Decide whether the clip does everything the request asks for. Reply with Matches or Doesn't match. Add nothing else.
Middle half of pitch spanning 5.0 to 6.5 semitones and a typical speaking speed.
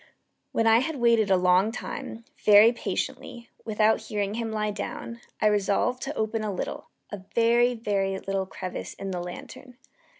Doesn't match